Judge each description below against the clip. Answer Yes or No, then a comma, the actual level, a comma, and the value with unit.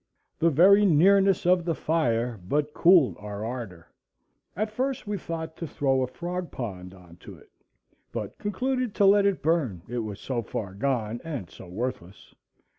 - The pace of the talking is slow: No, average, 170 wpm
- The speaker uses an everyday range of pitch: No, wide, 8.5 semitones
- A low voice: No, medium, 145 Hz